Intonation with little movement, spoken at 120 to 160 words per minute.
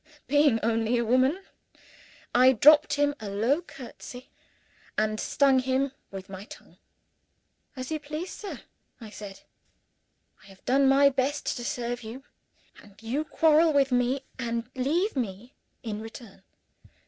No: average, 4.0 semitones; average, 140 wpm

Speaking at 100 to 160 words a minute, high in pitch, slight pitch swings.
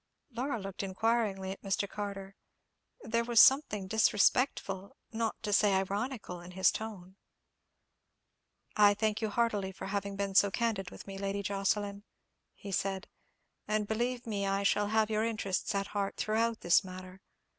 Yes: average, 155 wpm; high, 200 Hz; narrow, 2.2 semitones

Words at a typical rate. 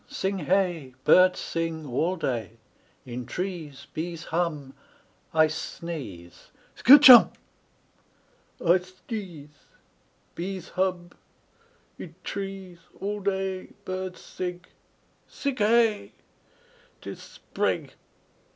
No: slow, 90 wpm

